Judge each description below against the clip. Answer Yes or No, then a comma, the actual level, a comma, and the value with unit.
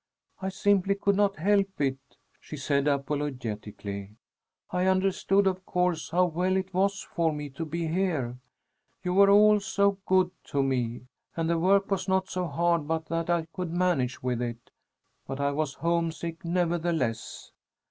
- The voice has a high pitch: No, medium, 170 Hz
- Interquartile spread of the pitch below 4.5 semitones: No, average, 4.9 semitones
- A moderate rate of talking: Yes, average, 160 wpm